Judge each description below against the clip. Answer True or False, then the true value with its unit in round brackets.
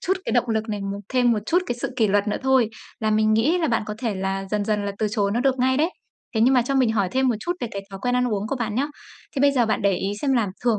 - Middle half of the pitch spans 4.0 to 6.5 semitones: False (3.6 semitones)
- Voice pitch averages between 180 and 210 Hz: False (225 Hz)